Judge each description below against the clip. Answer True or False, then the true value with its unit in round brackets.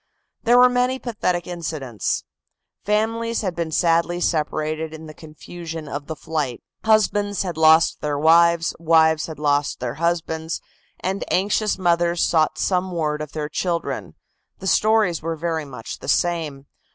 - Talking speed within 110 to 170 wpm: True (150 wpm)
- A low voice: False (165 Hz)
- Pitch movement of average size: True (3.0 semitones)